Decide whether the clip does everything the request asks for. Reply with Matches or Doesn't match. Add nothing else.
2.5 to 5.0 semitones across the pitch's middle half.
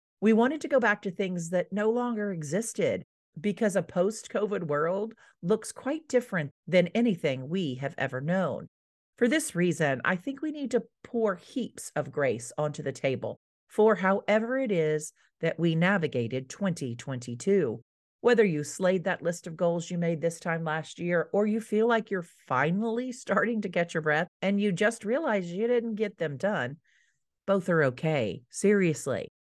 Doesn't match